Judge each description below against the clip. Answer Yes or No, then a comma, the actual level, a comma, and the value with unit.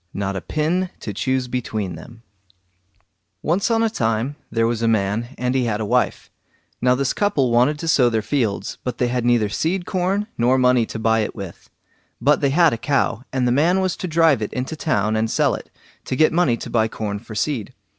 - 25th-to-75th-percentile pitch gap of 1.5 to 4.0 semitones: No, average, 5.2 semitones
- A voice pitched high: No, low, 125 Hz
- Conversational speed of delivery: No, fast, 215 wpm